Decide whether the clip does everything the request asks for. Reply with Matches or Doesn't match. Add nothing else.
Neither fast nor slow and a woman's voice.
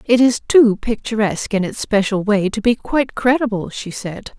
Matches